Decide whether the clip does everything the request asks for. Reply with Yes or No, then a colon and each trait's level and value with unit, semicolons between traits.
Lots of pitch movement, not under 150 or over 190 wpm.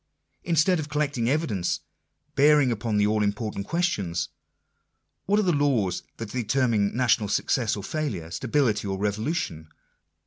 No: wide, 6.3 semitones; average, 140 wpm